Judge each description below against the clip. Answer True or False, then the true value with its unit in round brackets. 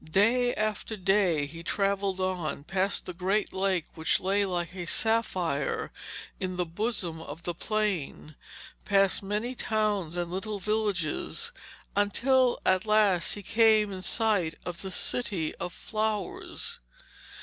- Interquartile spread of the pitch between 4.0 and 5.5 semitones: False (3.4 semitones)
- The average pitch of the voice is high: True (195 Hz)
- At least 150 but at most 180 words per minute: False (135 wpm)